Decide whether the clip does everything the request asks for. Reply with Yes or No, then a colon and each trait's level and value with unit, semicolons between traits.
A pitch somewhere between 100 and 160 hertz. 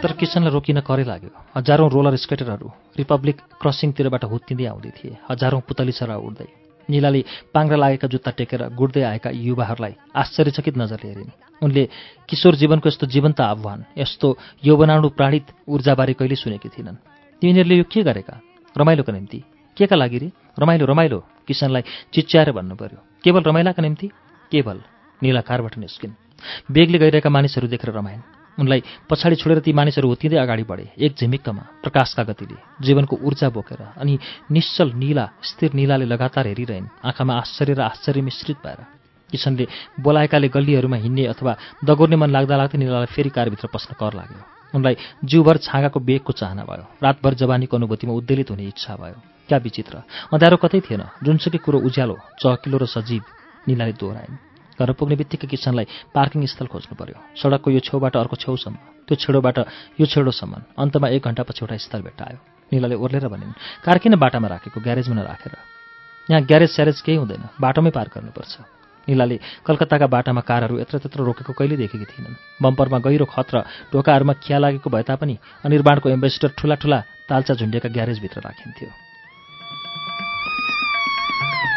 Yes: low, 135 Hz